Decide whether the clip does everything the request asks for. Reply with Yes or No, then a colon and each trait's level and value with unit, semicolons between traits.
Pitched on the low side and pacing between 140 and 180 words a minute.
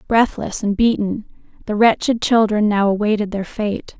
No: high, 210 Hz; average, 150 wpm